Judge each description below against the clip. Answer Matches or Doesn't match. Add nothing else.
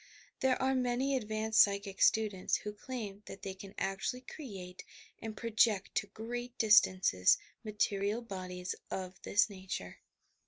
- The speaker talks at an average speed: Doesn't match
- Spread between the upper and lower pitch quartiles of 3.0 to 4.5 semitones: Matches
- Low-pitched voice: Doesn't match